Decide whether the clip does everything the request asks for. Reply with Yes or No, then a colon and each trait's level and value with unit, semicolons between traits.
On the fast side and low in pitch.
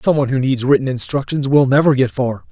Yes: fast, 215 wpm; low, 130 Hz